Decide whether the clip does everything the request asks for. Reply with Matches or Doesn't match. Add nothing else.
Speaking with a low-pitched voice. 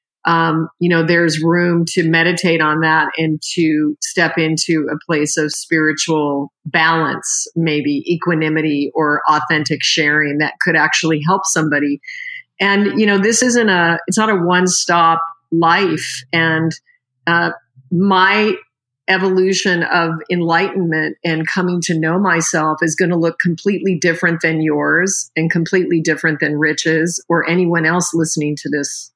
Doesn't match